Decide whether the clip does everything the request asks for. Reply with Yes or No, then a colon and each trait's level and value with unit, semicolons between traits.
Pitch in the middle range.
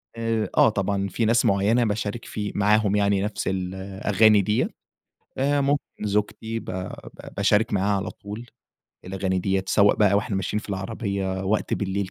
No: low, 100 Hz